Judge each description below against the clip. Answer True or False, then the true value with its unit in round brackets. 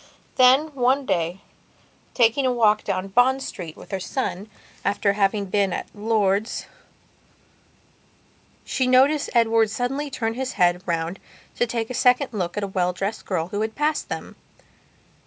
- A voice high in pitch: True (220 Hz)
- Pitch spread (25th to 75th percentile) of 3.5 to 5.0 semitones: True (4.6 semitones)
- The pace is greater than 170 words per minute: False (155 wpm)